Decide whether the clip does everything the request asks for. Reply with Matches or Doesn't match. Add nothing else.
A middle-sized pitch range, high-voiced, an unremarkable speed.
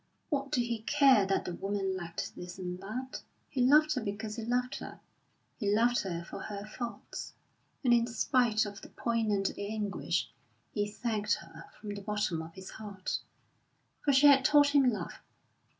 Matches